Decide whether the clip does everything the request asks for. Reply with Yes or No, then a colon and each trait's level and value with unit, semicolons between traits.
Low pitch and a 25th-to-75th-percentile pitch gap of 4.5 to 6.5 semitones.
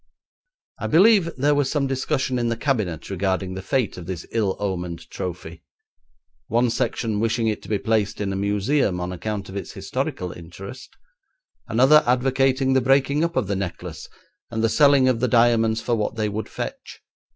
Yes: low, 115 Hz; average, 5.2 semitones